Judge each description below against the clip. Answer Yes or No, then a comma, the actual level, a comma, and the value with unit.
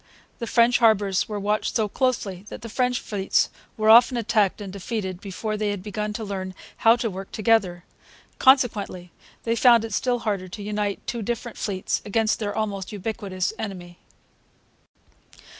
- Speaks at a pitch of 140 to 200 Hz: No, high, 210 Hz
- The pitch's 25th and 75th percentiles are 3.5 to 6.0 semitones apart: No, average, 2.8 semitones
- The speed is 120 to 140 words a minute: No, average, 160 wpm